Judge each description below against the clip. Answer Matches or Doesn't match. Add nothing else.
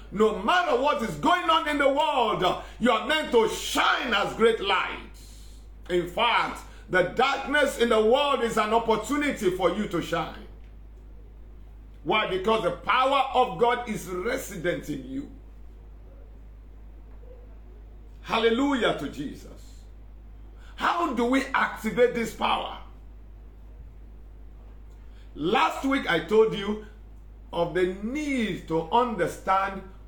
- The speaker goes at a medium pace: Doesn't match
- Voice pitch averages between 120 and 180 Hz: Doesn't match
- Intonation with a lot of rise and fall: Matches